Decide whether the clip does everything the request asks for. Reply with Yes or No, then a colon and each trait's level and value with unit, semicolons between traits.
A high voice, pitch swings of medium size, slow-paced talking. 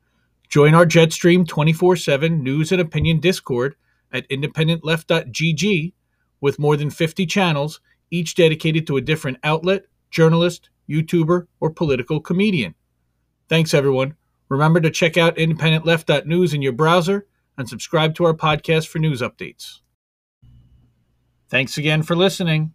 No: medium, 160 Hz; average, 3.2 semitones; slow, 130 wpm